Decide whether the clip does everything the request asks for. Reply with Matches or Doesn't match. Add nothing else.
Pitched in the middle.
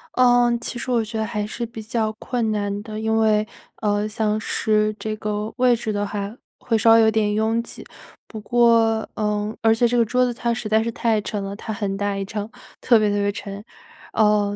Doesn't match